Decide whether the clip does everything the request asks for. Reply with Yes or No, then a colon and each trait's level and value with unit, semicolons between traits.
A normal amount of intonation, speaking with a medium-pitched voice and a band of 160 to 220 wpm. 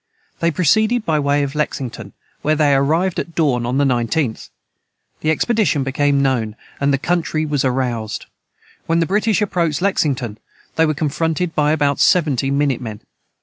Yes: average, 3.6 semitones; medium, 145 Hz; average, 165 wpm